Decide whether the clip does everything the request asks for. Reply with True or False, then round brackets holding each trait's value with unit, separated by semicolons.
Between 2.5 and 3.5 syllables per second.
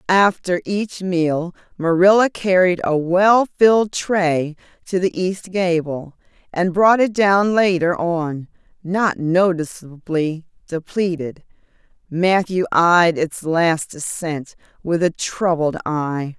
True (3.4 syllables/s)